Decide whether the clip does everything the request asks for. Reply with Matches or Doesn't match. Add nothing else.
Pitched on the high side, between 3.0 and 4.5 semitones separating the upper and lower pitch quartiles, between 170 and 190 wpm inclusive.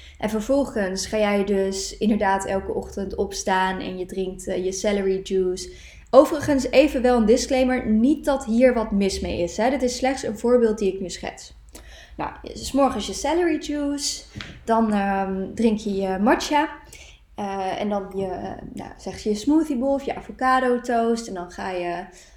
Doesn't match